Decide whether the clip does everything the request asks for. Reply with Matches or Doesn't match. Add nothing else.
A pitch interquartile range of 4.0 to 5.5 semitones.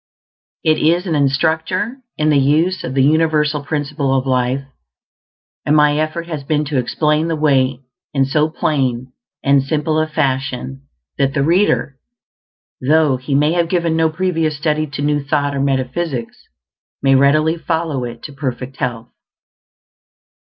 Doesn't match